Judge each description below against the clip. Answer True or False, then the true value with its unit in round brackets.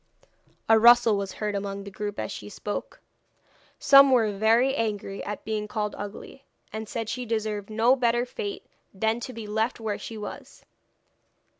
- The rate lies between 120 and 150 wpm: False (165 wpm)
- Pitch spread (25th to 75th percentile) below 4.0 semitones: True (2.4 semitones)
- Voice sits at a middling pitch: False (220 Hz)